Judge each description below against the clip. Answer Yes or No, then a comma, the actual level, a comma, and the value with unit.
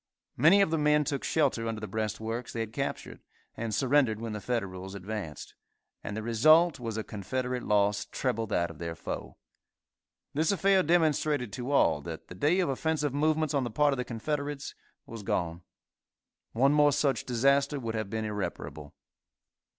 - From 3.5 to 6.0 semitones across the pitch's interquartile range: Yes, wide, 5.4 semitones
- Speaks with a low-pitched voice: Yes, low, 125 Hz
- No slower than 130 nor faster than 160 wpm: No, average, 175 wpm